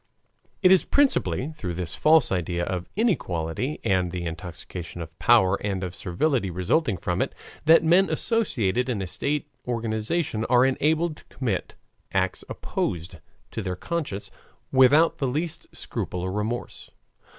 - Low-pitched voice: Yes, low, 110 Hz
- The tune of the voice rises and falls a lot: Yes, wide, 9.0 semitones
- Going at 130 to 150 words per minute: Yes, average, 145 wpm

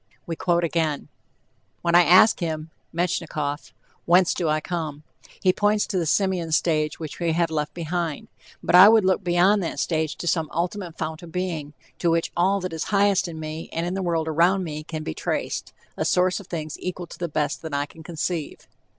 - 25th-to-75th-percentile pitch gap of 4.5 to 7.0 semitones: No, narrow, 2.4 semitones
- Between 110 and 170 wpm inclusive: No, fast, 205 wpm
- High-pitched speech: No, medium, 170 Hz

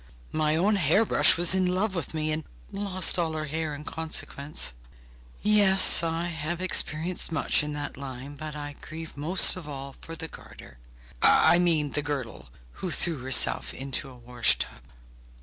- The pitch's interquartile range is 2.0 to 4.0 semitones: Yes, average, 3.2 semitones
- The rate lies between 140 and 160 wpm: No, average, 170 wpm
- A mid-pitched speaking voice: Yes, medium, 155 Hz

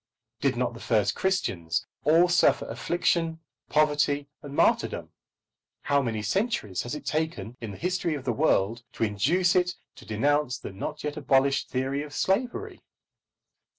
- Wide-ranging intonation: Yes, wide, 6.2 semitones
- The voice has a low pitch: No, medium, 145 Hz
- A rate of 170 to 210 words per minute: No, average, 150 wpm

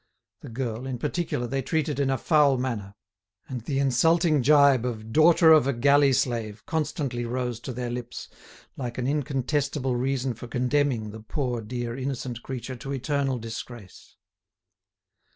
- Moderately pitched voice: No, low, 130 Hz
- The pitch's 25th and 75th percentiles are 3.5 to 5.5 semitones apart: No, average, 2.8 semitones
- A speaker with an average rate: Yes, average, 150 wpm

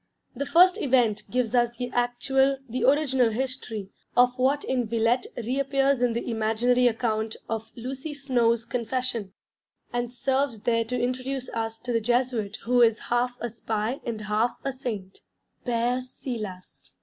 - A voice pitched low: No, high, 245 Hz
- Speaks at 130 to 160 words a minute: Yes, average, 150 wpm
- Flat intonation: Yes, narrow, 2.2 semitones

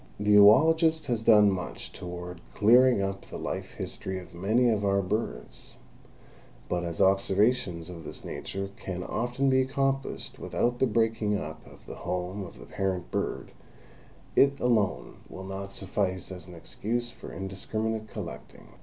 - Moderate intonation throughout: Yes, average, 4.2 semitones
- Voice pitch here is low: Yes, low, 100 Hz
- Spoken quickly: No, average, 155 wpm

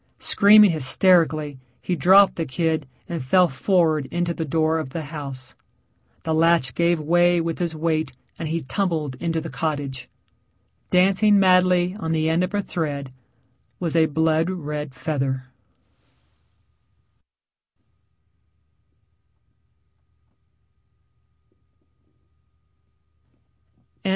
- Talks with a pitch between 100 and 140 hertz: No, medium, 160 Hz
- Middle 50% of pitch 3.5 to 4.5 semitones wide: No, average, 2.8 semitones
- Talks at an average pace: No, slow, 100 wpm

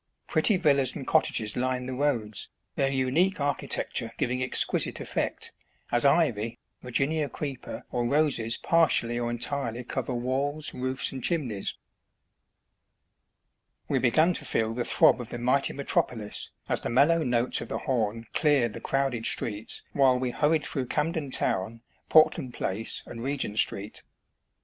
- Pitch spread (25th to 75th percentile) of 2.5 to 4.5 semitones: Yes, average, 3.4 semitones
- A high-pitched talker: No, low, 130 Hz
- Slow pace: No, average, 150 wpm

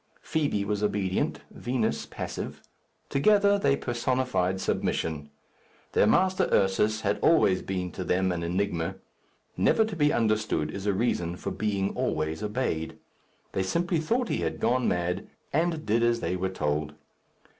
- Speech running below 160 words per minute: Yes, average, 145 wpm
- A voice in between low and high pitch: No, low, 105 Hz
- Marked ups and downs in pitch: Yes, wide, 6.2 semitones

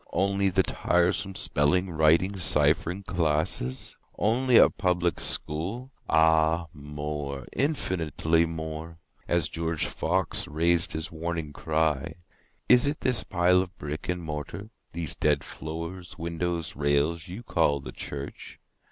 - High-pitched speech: No, very low, 85 Hz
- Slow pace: Yes, slow, 105 wpm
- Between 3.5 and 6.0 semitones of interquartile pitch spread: No, average, 2.9 semitones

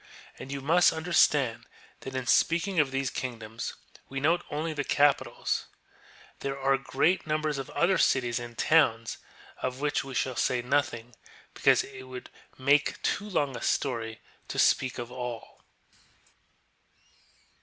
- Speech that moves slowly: No, average, 145 wpm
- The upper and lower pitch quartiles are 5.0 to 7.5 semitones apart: No, average, 3.2 semitones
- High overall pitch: No, low, 135 Hz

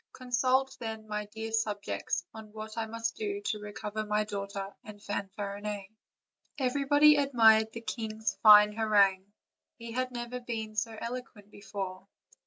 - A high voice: Yes, high, 220 Hz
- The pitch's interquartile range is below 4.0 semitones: Yes, narrow, 2.4 semitones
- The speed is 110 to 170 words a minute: Yes, average, 140 wpm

